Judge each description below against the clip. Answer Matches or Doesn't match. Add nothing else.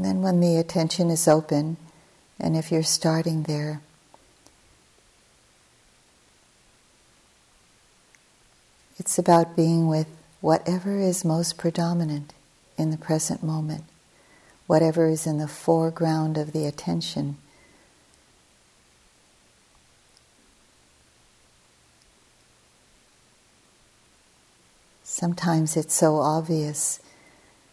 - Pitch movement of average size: Doesn't match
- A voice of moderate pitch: Matches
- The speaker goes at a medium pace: Doesn't match